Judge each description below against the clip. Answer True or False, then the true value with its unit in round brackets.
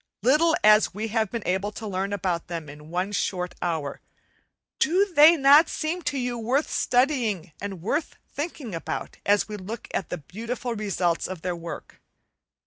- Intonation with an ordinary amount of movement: False (6.6 semitones)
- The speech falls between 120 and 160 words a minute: False (170 wpm)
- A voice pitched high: True (210 Hz)